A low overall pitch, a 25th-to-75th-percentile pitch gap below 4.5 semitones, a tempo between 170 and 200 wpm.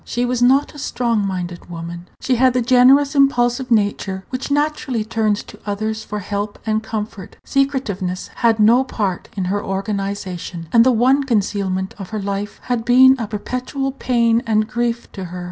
No: high, 220 Hz; average, 4.0 semitones; average, 175 wpm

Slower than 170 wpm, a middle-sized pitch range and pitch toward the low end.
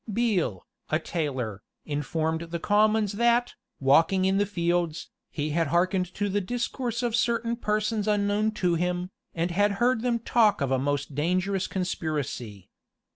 No: average, 150 wpm; average, 5.0 semitones; medium, 185 Hz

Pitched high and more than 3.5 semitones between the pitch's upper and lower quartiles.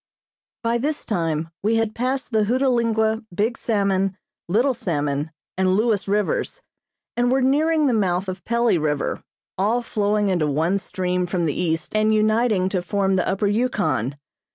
Yes: high, 205 Hz; average, 4.5 semitones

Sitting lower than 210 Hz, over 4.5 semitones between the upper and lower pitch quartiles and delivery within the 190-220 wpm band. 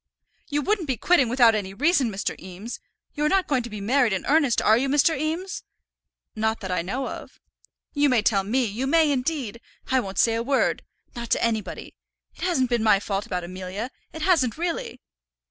No: high, 245 Hz; wide, 5.6 semitones; average, 200 wpm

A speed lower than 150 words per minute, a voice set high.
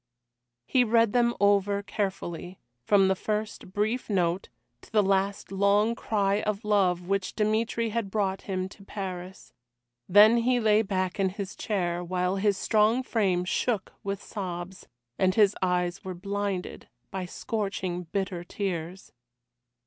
Yes: average, 140 wpm; high, 195 Hz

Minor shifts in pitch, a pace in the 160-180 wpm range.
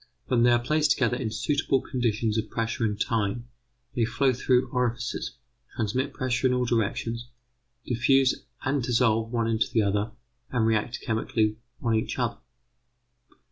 No: narrow, 2.1 semitones; average, 145 wpm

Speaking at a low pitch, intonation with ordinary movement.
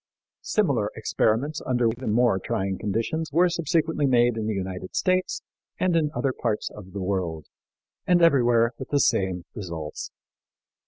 No: low, 120 Hz; wide, 7.4 semitones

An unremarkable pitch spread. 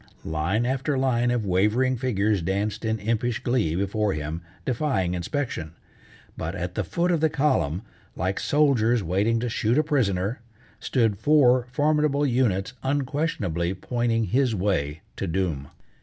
No: wide, 5.7 semitones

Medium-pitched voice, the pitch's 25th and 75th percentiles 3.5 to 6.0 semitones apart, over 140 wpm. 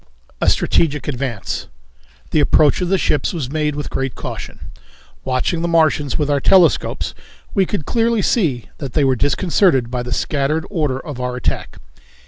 Yes: medium, 150 Hz; average, 4.2 semitones; average, 165 wpm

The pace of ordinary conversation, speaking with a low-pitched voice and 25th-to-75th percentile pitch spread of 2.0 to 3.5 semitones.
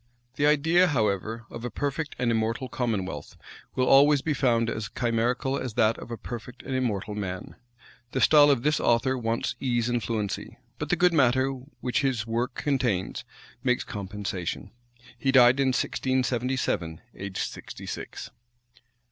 Yes: average, 155 wpm; low, 120 Hz; average, 3.1 semitones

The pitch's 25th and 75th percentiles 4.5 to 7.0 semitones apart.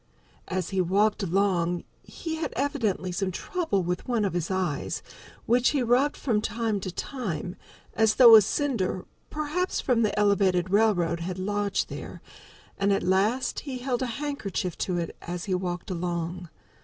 Yes: average, 5.0 semitones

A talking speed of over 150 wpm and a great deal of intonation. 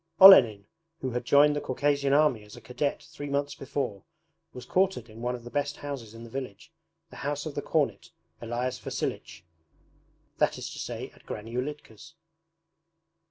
No: average, 170 wpm; average, 3.8 semitones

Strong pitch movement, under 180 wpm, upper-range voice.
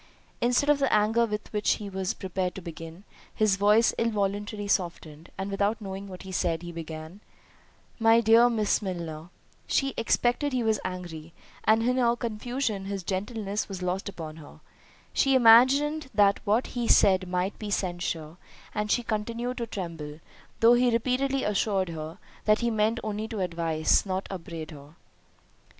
No: average, 4.3 semitones; average, 165 wpm; high, 205 Hz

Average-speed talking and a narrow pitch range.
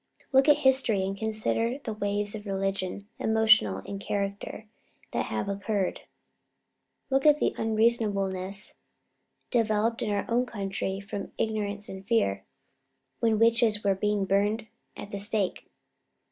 No: slow, 130 wpm; narrow, 2.3 semitones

